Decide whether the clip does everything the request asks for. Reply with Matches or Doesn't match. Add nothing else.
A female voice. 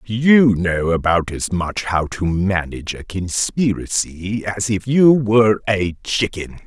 Doesn't match